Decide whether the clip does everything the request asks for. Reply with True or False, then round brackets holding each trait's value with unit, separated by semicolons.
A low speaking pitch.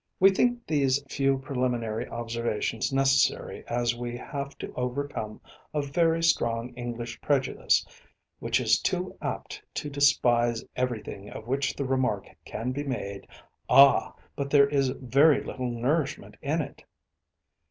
True (130 Hz)